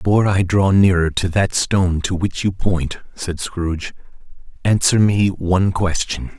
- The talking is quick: No, average, 160 wpm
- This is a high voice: No, very low, 95 Hz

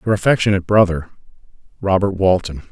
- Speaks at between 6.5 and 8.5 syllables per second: Yes, 6.6 syllables/s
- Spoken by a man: Yes, male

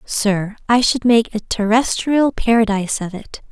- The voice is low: No, high, 225 Hz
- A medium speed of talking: Yes, average, 155 wpm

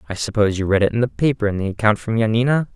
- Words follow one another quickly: Yes, fast, 285 wpm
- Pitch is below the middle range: Yes, low, 110 Hz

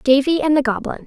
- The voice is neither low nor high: No, very high, 280 Hz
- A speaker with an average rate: No, fast, 225 wpm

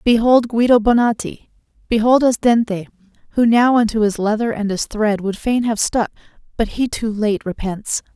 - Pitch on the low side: No, high, 225 Hz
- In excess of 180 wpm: No, average, 160 wpm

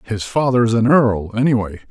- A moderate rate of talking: Yes, average, 190 wpm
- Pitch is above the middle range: No, low, 115 Hz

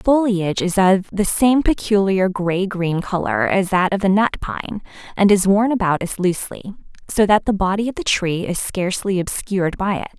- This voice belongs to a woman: Yes, female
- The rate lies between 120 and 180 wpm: No, average, 200 wpm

